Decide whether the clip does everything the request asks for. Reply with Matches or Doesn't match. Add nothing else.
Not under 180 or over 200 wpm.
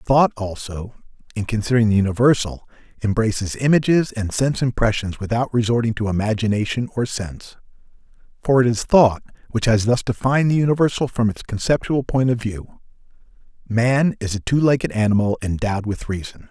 Doesn't match